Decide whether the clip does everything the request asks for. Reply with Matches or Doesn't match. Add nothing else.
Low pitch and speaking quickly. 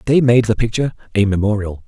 Doesn't match